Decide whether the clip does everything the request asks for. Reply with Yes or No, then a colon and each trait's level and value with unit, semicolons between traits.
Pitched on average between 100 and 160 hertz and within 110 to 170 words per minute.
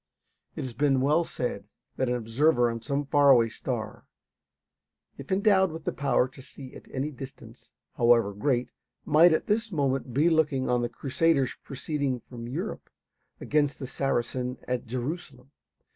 Yes: low, 135 Hz; average, 160 wpm